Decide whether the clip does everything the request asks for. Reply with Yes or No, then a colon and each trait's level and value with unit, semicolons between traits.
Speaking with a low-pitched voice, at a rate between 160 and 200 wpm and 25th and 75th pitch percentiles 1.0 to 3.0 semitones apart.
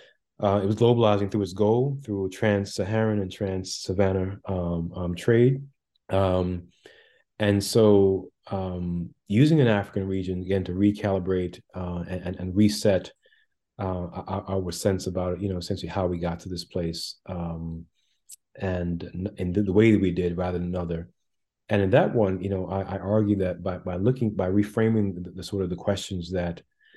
Yes: very low, 95 Hz; average, 170 wpm; narrow, 2.4 semitones